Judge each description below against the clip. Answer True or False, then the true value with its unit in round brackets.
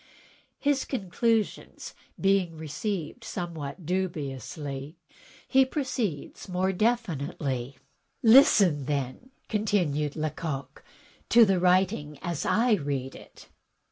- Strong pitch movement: True (6.4 semitones)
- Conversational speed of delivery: False (90 wpm)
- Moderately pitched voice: True (175 Hz)